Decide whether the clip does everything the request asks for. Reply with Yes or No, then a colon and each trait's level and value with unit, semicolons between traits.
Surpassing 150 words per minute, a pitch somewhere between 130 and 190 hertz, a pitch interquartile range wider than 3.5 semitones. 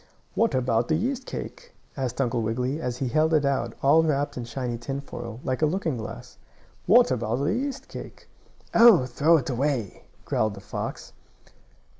Yes: average, 170 wpm; low, 135 Hz; average, 4.7 semitones